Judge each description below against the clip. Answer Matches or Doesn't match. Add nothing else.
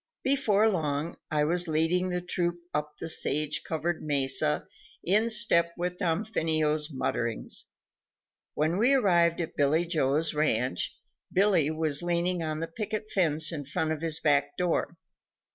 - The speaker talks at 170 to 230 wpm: Doesn't match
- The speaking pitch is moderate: Matches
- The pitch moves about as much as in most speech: Matches